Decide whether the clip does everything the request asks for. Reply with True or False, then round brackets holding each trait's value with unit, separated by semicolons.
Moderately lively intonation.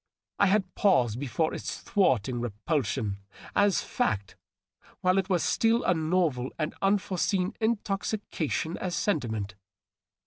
False (8.0 semitones)